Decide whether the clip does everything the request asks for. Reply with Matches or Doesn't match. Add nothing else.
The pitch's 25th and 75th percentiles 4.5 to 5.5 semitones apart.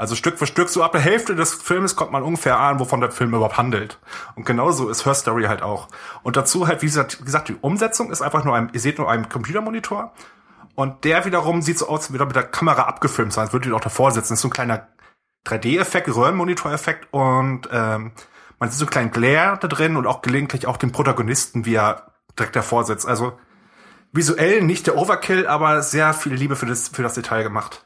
Matches